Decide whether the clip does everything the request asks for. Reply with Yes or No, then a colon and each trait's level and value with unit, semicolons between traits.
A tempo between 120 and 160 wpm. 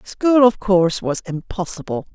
Yes: average, 140 wpm